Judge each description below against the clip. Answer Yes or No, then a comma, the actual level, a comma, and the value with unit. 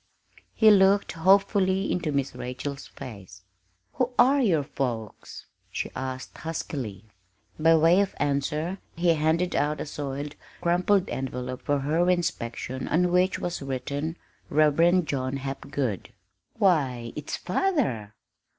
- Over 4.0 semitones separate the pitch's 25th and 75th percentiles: Yes, average, 5.3 semitones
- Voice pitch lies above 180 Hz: No, medium, 150 Hz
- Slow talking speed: Yes, slow, 125 wpm